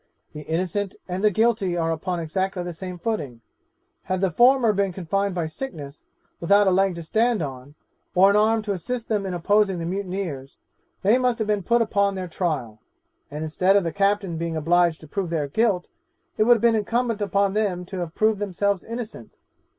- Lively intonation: No, average, 3.8 semitones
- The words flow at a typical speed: Yes, average, 195 wpm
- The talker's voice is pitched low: No, high, 190 Hz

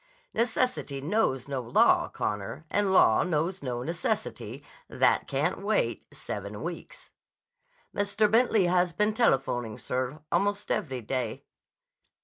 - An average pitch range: No, wide, 8.1 semitones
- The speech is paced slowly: Yes, slow, 120 wpm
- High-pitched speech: No, medium, 170 Hz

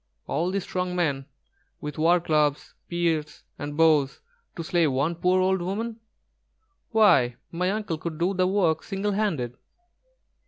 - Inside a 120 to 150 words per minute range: Yes, slow, 135 wpm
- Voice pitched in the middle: Yes, medium, 170 Hz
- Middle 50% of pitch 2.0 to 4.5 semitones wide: Yes, average, 3.6 semitones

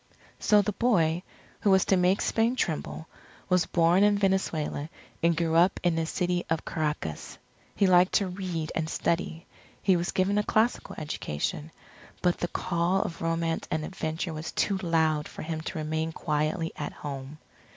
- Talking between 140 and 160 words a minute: No, average, 170 wpm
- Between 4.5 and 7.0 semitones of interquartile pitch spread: No, average, 3.0 semitones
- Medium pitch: Yes, medium, 170 Hz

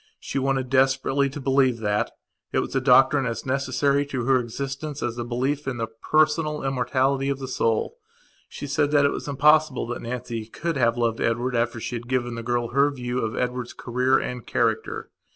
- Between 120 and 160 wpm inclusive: No, average, 195 wpm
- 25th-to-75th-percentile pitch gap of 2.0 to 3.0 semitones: Yes, narrow, 2.5 semitones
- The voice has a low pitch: Yes, low, 130 Hz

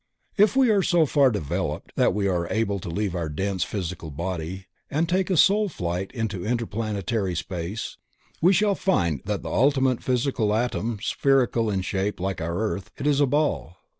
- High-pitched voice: No, low, 105 Hz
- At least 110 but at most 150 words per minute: No, average, 185 wpm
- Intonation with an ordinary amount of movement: No, wide, 7.1 semitones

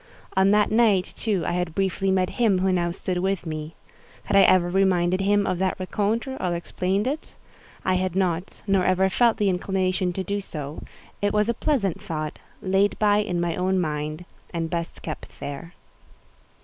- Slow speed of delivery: No, average, 185 wpm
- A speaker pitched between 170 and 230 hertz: Yes, medium, 185 Hz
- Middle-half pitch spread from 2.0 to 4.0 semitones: Yes, narrow, 2.4 semitones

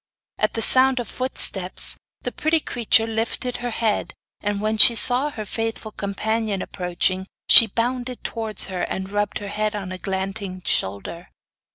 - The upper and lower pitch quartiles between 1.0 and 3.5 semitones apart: Yes, average, 3.2 semitones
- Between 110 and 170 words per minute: Yes, average, 155 wpm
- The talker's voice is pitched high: Yes, high, 215 Hz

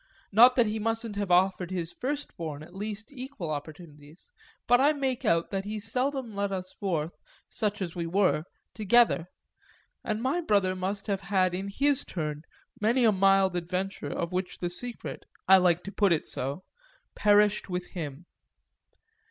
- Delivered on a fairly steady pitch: No, average, 3.9 semitones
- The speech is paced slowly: No, average, 165 wpm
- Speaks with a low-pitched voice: No, high, 195 Hz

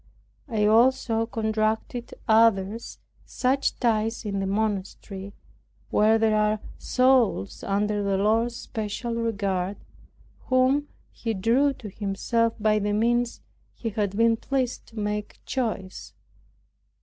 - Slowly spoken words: Yes, slow, 115 wpm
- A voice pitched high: Yes, high, 220 Hz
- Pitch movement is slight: Yes, narrow, 2.2 semitones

